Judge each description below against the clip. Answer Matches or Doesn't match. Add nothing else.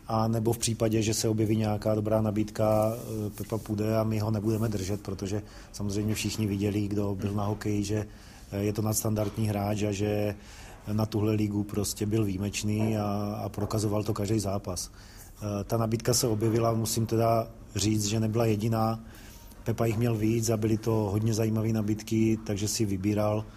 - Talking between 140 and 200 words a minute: Matches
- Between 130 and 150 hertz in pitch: Doesn't match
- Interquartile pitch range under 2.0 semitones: Matches